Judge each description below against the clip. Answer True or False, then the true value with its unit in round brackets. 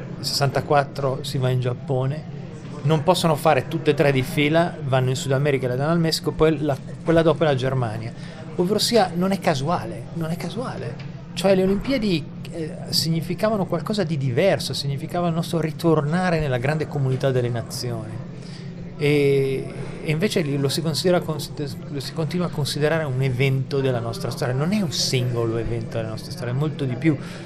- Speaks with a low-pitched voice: False (155 Hz)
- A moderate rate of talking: False (180 wpm)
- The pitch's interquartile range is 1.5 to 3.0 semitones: False (3.4 semitones)